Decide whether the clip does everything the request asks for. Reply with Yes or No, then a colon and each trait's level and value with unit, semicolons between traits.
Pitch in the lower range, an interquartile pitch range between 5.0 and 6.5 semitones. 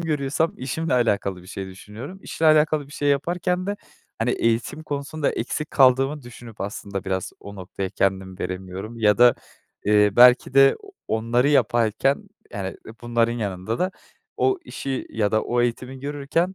Yes: low, 120 Hz; wide, 5.6 semitones